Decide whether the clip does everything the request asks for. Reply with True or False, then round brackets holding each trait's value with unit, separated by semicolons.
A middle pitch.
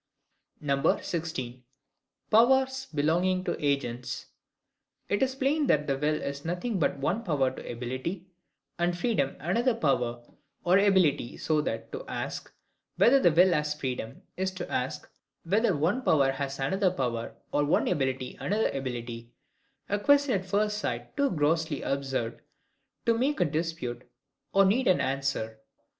True (160 Hz)